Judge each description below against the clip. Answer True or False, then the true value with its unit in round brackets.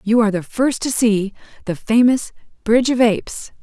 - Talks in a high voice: True (225 Hz)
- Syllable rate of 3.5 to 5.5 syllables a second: True (5.0 syllables/s)